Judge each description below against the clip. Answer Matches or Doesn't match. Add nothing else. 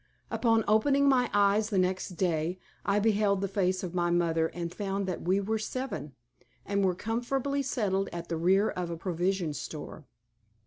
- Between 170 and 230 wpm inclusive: Matches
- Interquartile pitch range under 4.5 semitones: Matches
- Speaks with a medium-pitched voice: Doesn't match